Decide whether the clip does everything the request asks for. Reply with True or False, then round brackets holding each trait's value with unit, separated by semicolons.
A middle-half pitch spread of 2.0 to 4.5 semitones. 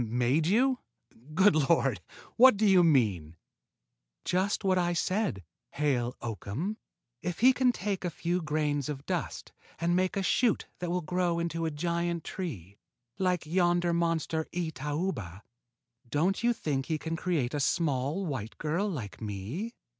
False (4.9 semitones)